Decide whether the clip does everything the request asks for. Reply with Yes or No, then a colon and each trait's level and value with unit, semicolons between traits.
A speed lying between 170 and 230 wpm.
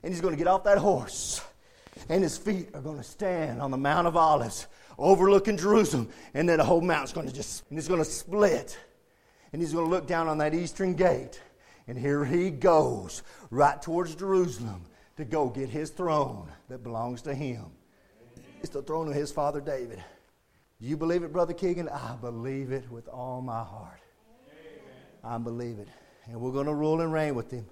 Yes: average, 200 wpm